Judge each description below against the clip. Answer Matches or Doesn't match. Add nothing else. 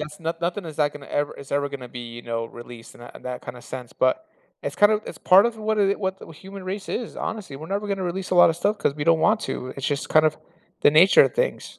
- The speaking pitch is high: Doesn't match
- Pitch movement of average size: Doesn't match